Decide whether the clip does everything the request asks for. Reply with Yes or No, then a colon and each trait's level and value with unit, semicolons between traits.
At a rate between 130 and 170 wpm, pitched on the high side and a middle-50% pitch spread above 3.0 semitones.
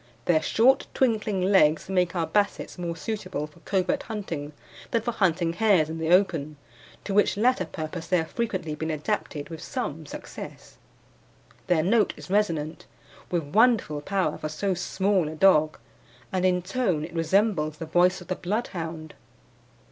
No: average, 160 wpm; medium, 180 Hz; average, 4.1 semitones